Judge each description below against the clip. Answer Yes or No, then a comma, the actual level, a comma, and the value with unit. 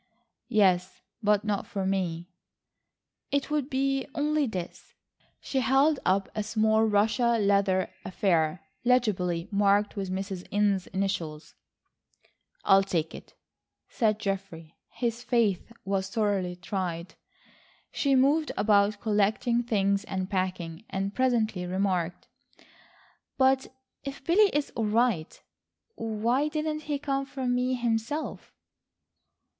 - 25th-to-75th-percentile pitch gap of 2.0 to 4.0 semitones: No, average, 4.8 semitones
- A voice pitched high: Yes, high, 210 Hz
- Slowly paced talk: Yes, slow, 120 wpm